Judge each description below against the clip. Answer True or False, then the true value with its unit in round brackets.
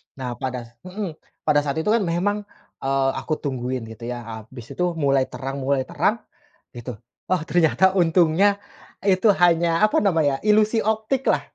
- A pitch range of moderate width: False (6.2 semitones)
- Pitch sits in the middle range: True (160 Hz)